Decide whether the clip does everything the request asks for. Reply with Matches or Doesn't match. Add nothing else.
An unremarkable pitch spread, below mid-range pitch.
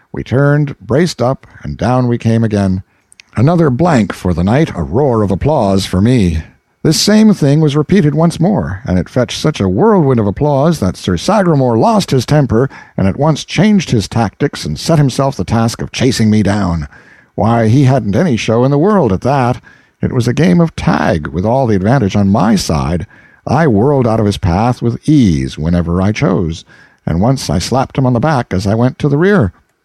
Doesn't match